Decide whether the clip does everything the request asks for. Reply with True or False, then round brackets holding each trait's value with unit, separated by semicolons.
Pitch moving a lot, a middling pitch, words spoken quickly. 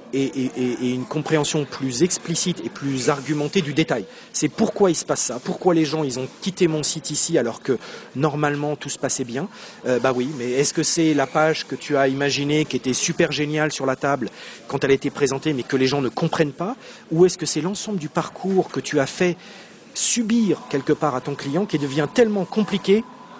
False (4.7 semitones; 155 Hz; 225 wpm)